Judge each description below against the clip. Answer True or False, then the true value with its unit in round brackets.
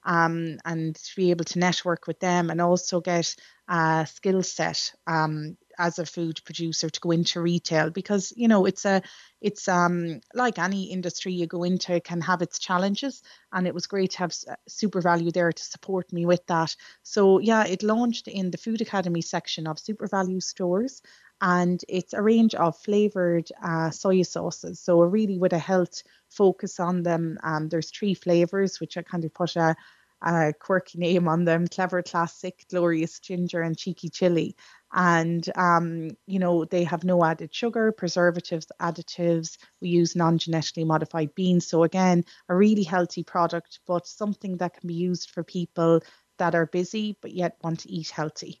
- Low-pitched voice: False (175 Hz)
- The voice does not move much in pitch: True (2.0 semitones)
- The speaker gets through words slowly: False (185 wpm)